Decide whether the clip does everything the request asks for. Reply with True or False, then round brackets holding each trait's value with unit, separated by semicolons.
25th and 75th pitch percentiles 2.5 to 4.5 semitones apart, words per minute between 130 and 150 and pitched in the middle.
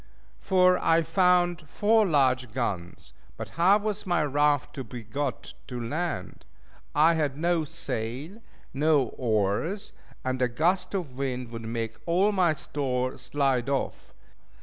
False (5.6 semitones; 140 wpm; 145 Hz)